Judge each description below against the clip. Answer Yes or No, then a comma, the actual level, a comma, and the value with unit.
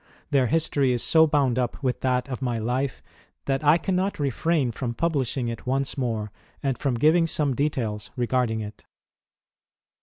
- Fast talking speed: No, average, 160 wpm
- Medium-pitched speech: No, low, 130 Hz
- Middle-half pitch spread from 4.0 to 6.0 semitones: No, average, 3.5 semitones